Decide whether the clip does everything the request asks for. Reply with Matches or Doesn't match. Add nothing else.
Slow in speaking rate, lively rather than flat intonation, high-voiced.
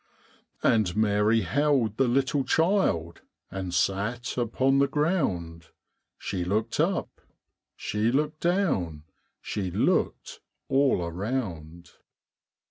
Doesn't match